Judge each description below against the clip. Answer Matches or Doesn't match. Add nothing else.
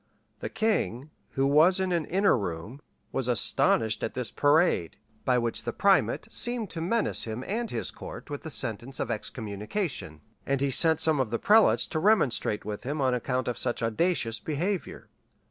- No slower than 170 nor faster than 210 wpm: Matches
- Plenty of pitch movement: Matches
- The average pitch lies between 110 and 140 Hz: Matches